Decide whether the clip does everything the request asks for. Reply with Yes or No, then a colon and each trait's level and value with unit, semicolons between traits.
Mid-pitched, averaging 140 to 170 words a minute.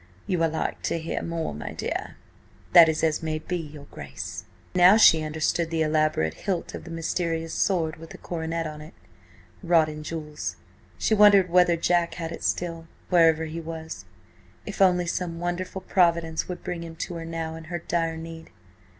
No: medium, 165 Hz; average, 185 wpm